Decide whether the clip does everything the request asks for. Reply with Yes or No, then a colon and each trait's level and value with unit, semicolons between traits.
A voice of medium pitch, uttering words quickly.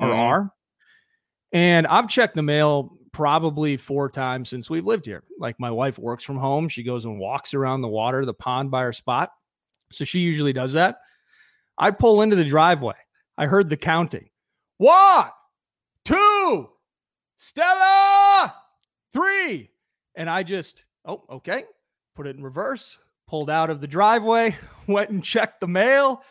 No: medium, 165 Hz; average, 155 wpm